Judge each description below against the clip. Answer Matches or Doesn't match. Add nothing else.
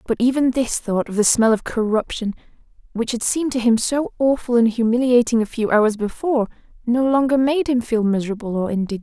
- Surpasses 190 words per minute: Matches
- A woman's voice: Matches